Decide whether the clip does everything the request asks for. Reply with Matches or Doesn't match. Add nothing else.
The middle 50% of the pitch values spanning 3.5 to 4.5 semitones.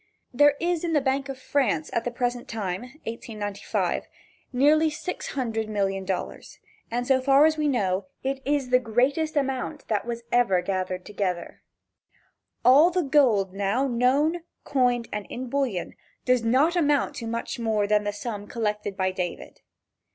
Doesn't match